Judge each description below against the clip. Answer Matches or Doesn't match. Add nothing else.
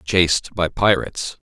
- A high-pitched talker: Doesn't match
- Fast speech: Doesn't match